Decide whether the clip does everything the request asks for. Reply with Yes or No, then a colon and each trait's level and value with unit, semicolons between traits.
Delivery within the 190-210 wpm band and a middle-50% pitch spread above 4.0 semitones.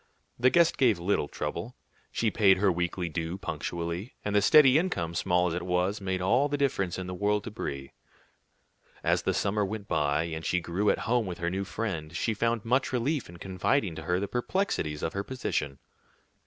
Yes: average, 200 wpm; average, 4.9 semitones